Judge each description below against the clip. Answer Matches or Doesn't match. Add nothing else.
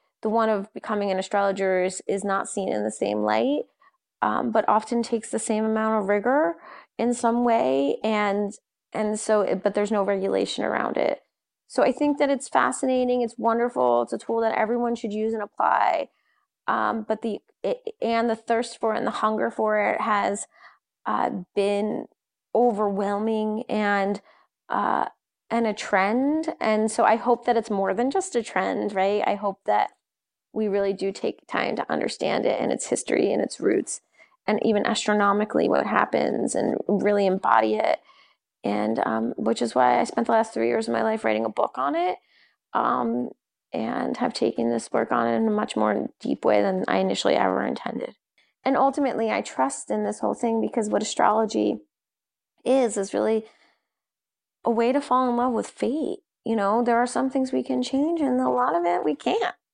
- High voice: Matches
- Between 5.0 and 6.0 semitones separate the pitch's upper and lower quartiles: Doesn't match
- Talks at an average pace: Matches